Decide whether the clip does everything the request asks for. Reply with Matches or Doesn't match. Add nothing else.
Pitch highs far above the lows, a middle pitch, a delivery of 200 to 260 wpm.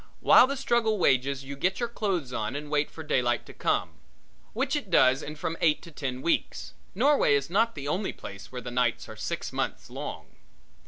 Matches